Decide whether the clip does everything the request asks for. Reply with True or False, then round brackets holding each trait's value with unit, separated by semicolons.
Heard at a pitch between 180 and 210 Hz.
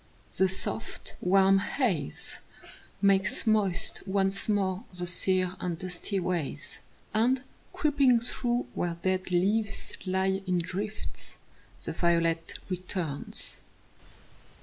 True (190 Hz)